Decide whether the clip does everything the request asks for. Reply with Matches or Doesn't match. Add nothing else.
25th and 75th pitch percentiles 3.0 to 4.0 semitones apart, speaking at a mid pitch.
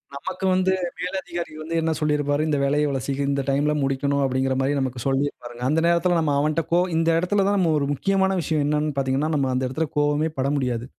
Matches